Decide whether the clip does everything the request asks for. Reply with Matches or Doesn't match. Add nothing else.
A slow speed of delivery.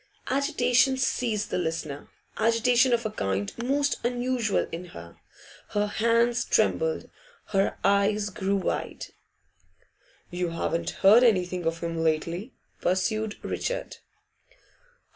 Matches